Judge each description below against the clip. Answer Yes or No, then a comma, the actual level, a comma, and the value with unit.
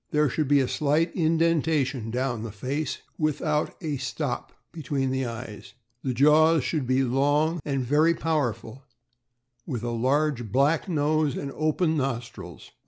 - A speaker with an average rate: Yes, average, 145 wpm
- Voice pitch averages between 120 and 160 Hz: Yes, medium, 140 Hz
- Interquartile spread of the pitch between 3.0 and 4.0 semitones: Yes, average, 3.5 semitones